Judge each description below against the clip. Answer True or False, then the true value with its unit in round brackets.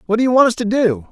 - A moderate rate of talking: False (375 wpm)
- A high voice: True (220 Hz)